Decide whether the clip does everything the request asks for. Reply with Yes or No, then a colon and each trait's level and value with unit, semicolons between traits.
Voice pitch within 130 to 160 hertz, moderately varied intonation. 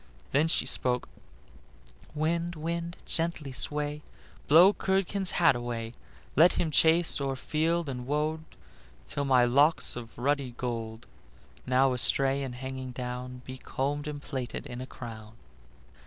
Yes: medium, 140 Hz; average, 4.2 semitones